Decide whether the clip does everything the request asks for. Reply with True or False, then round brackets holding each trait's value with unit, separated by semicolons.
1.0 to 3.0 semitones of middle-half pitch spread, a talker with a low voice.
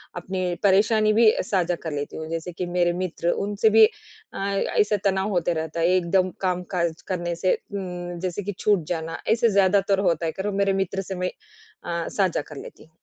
False (2.6 semitones; 185 Hz)